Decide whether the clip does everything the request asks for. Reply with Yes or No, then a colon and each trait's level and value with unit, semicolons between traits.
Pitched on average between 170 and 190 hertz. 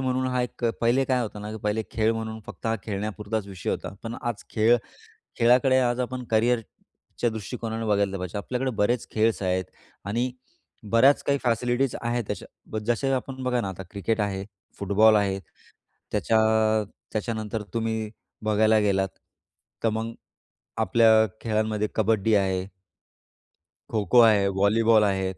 No: low, 110 Hz